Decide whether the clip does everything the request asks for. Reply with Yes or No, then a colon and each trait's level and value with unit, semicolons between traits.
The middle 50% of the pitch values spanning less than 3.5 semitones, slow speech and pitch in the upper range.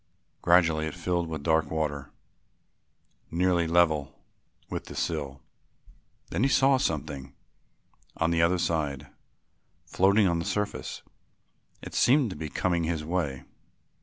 No: average, 2.8 semitones; slow, 130 wpm; very low, 85 Hz